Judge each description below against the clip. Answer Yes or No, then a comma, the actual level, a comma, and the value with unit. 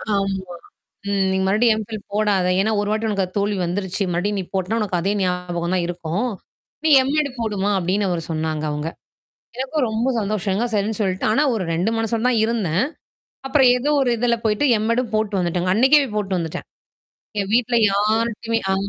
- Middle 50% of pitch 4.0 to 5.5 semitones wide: No, average, 3.5 semitones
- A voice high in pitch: Yes, high, 205 Hz